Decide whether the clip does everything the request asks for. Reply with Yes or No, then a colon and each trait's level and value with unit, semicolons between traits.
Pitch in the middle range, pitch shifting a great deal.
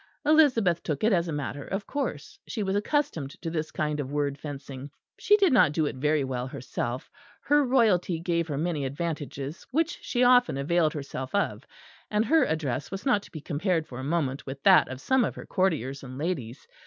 Yes: medium, 160 Hz; wide, 6.5 semitones